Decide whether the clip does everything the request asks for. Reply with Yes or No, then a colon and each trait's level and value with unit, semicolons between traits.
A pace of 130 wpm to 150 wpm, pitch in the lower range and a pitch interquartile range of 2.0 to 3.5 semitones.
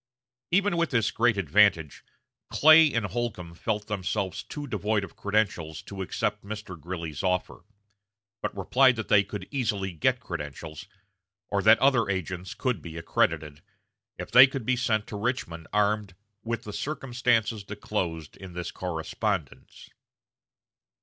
No: average, 140 wpm; low, 105 Hz; average, 4.4 semitones